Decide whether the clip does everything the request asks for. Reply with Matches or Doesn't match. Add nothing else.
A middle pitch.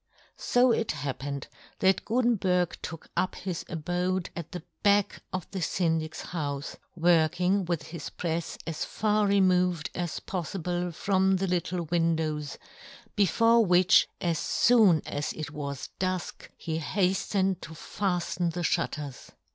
Matches